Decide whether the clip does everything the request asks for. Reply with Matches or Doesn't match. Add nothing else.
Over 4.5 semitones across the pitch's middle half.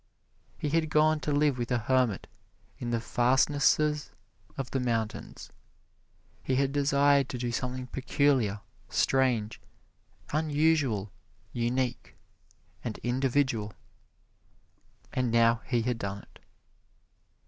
Doesn't match